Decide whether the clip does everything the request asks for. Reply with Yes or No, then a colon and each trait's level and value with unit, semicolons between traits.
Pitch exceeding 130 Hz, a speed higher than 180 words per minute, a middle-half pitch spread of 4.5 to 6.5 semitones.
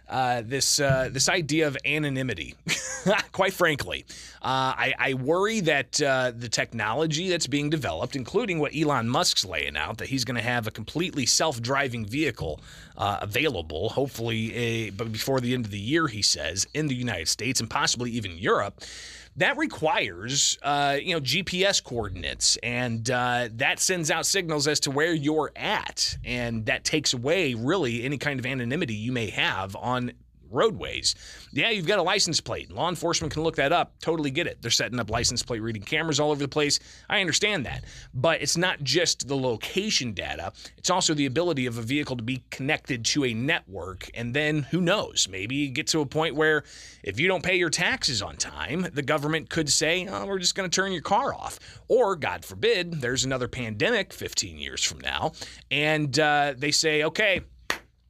Yes: medium, 140 Hz; average, 190 wpm; average, 4.8 semitones